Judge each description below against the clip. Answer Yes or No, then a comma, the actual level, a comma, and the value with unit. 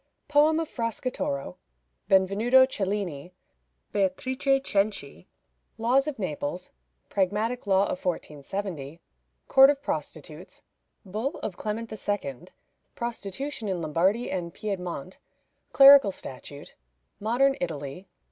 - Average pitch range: No, wide, 5.8 semitones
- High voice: Yes, high, 200 Hz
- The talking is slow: Yes, slow, 100 wpm